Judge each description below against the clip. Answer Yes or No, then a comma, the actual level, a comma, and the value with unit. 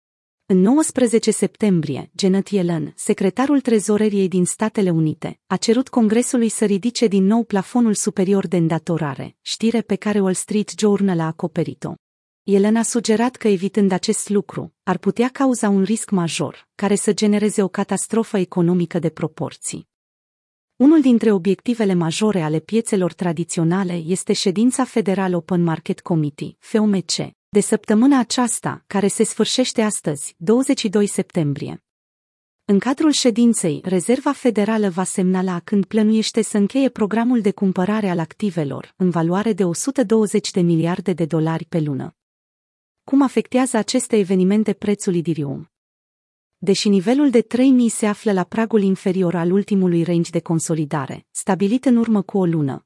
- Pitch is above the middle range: Yes, high, 200 Hz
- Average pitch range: Yes, average, 4.1 semitones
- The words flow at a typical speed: Yes, average, 140 wpm